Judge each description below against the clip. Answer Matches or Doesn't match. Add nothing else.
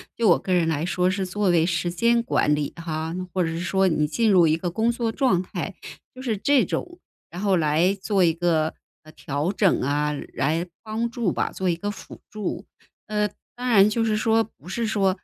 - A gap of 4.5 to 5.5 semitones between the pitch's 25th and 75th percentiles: Matches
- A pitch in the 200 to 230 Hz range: Doesn't match